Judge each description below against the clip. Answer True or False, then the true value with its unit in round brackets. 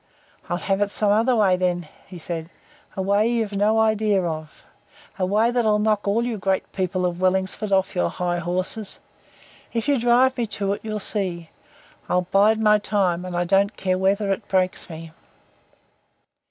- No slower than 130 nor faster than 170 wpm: False (180 wpm)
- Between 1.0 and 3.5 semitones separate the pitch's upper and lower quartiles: True (2.9 semitones)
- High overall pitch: True (195 Hz)